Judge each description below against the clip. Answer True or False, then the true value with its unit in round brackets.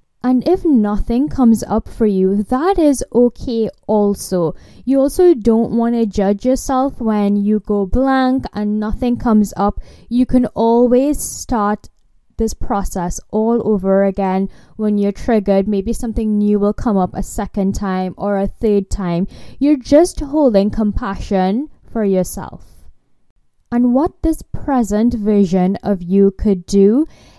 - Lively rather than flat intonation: False (3.7 semitones)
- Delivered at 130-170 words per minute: True (145 wpm)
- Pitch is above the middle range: True (215 Hz)